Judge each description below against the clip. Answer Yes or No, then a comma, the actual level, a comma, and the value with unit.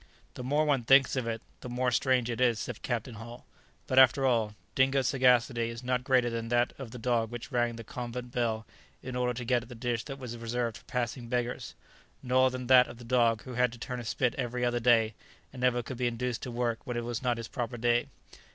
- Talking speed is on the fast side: Yes, fast, 245 wpm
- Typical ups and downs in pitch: No, narrow, 1.3 semitones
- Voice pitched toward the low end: Yes, low, 120 Hz